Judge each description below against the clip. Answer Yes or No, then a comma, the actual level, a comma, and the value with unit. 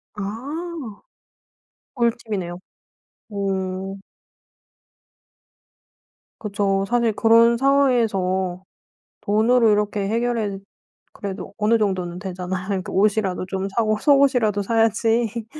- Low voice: No, high, 210 Hz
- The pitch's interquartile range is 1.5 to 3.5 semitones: Yes, average, 3.2 semitones